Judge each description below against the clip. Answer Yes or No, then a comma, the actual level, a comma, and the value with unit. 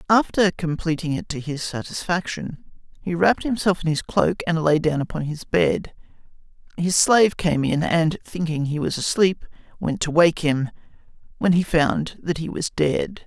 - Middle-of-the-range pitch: Yes, medium, 160 Hz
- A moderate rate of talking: Yes, average, 170 wpm